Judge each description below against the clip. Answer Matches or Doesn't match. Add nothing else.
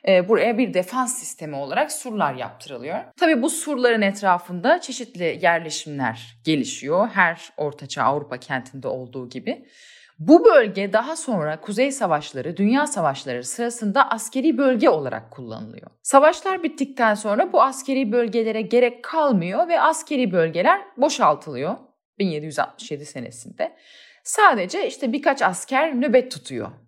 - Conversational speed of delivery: Matches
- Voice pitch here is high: Matches